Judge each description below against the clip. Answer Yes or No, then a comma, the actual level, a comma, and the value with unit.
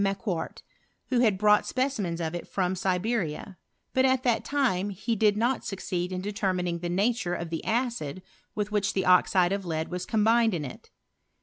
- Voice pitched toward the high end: Yes, high, 195 Hz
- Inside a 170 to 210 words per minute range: Yes, average, 180 wpm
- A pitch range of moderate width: Yes, average, 4.1 semitones